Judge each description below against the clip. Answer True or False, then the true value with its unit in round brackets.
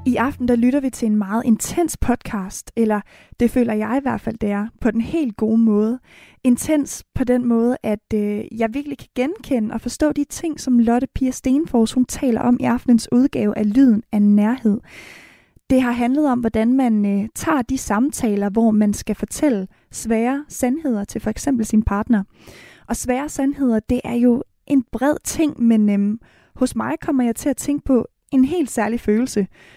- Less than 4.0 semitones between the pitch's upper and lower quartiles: True (3.2 semitones)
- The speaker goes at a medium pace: True (190 wpm)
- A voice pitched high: True (240 Hz)